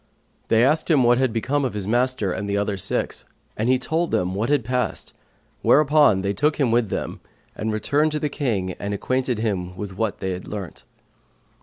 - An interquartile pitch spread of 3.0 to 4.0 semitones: No, average, 5.0 semitones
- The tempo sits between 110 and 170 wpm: No, average, 200 wpm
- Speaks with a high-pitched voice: No, low, 115 Hz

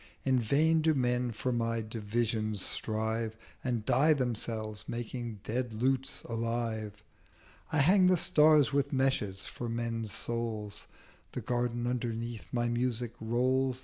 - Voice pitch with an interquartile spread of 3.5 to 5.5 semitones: No, narrow, 2.6 semitones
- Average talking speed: No, slow, 130 wpm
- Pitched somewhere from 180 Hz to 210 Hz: No, low, 120 Hz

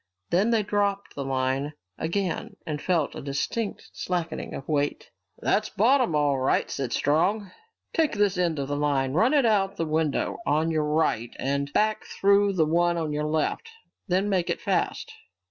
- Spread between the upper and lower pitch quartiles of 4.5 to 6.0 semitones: Yes, wide, 5.5 semitones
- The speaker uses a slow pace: No, average, 180 wpm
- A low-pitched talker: No, medium, 165 Hz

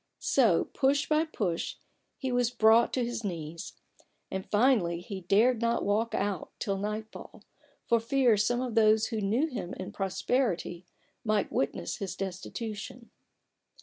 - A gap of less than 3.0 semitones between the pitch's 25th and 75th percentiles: No, average, 3.9 semitones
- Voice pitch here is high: Yes, high, 220 Hz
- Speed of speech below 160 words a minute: Yes, average, 145 wpm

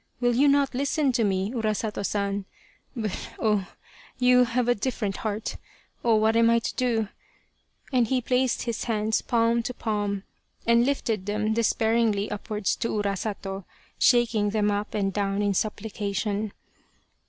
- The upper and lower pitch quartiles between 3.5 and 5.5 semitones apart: No, narrow, 2.5 semitones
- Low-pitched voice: No, high, 220 Hz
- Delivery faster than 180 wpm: No, average, 155 wpm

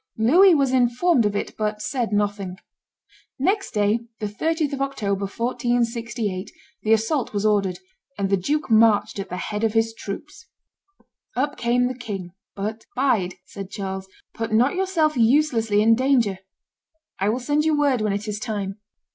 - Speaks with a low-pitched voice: No, high, 225 Hz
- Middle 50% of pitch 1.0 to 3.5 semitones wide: No, average, 4.3 semitones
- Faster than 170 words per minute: No, average, 165 wpm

